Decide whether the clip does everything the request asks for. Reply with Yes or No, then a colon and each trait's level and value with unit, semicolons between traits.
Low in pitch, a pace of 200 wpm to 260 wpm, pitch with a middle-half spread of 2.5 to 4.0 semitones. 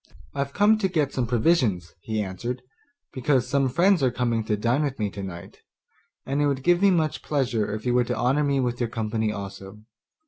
No: low, 125 Hz; fast, 205 wpm; average, 4.8 semitones